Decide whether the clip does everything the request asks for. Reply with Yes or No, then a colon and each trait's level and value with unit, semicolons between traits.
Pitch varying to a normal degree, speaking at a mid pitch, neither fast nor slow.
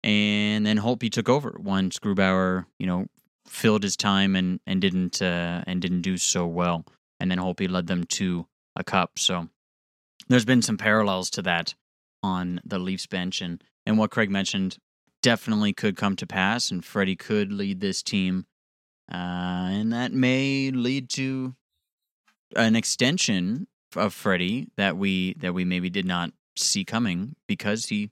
No: average, 3.8 semitones; very low, 95 Hz; average, 165 wpm